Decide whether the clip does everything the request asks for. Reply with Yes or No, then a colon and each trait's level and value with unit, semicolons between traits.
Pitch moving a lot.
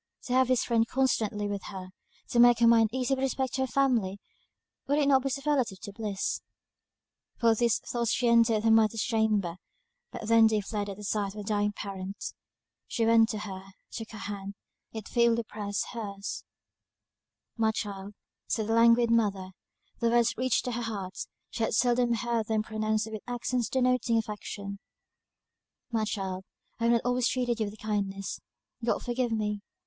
No: narrow, 2.6 semitones